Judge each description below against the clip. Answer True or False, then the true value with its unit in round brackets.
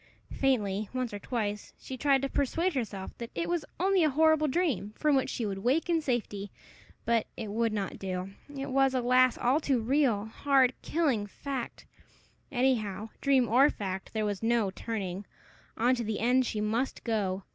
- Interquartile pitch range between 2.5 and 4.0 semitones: False (4.6 semitones)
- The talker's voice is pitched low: False (240 Hz)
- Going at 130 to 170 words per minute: False (180 wpm)